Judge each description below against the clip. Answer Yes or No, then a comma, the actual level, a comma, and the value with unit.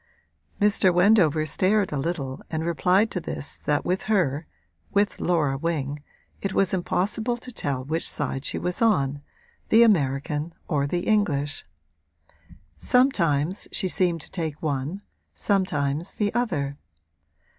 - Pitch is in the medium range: Yes, medium, 170 Hz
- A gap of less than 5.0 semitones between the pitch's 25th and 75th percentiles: No, wide, 5.5 semitones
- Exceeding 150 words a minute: No, slow, 135 wpm